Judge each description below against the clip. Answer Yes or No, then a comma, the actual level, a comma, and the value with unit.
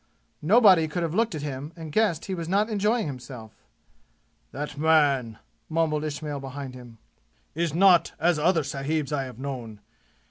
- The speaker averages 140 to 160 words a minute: Yes, average, 155 wpm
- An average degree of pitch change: Yes, average, 3.9 semitones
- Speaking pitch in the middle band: Yes, medium, 155 Hz